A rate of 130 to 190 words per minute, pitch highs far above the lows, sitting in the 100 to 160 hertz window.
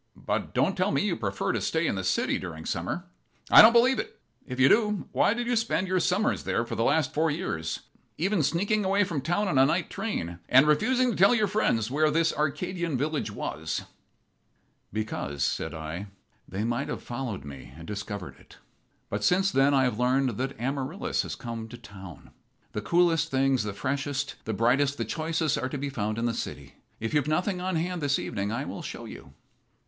No: fast, 205 wpm; wide, 7.7 semitones; medium, 140 Hz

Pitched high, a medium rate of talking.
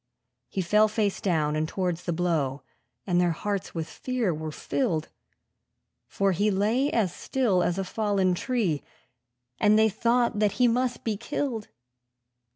Yes: high, 200 Hz; average, 155 wpm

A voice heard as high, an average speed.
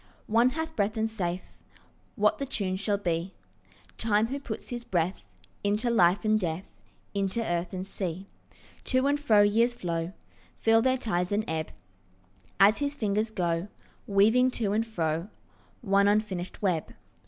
Yes: high, 205 Hz; average, 155 wpm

